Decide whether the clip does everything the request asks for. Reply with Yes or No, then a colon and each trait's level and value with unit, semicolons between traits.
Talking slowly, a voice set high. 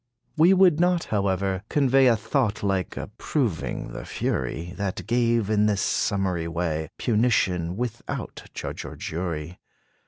No: slow, 130 wpm; low, 105 Hz